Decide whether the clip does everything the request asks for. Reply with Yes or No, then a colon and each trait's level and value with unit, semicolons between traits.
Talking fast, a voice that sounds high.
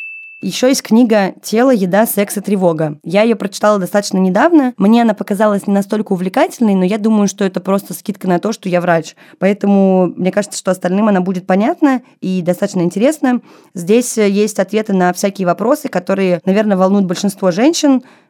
Yes: fast, 175 wpm; high, 200 Hz